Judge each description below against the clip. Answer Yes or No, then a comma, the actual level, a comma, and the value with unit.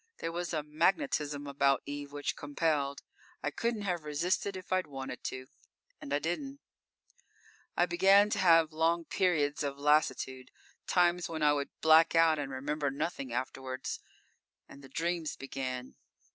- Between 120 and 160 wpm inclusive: Yes, average, 150 wpm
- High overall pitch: No, medium, 150 Hz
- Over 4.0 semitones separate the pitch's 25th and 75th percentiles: No, average, 3.6 semitones